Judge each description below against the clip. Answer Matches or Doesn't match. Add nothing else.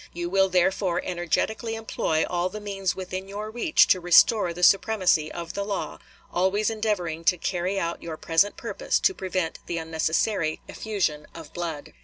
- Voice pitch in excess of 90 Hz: Matches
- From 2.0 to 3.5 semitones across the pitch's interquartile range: Matches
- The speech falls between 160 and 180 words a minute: Matches